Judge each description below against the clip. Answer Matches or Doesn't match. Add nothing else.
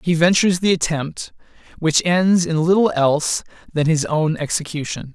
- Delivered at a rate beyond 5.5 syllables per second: Doesn't match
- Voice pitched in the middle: Matches